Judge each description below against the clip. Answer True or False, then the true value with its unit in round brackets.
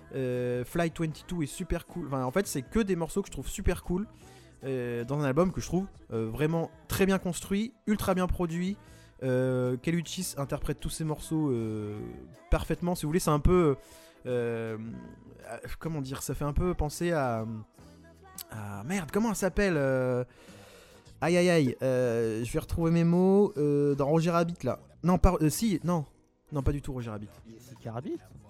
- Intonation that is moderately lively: False (6.3 semitones)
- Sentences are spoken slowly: False (185 wpm)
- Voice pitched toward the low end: False (145 Hz)